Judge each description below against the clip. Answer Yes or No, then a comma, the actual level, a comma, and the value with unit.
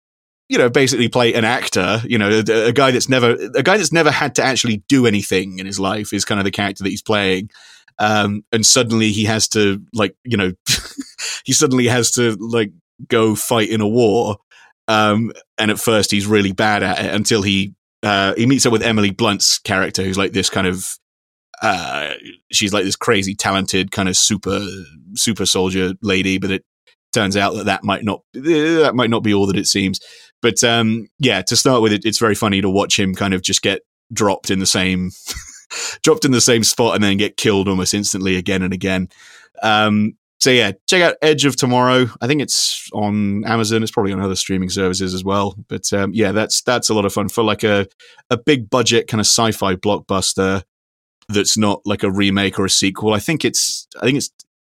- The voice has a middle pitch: No, low, 105 Hz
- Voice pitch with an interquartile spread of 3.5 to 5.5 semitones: No, average, 3.1 semitones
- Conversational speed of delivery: No, fast, 210 wpm